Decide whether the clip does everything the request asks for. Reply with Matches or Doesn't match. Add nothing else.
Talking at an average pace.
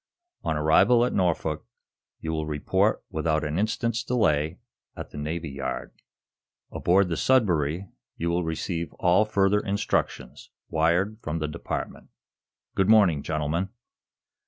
Doesn't match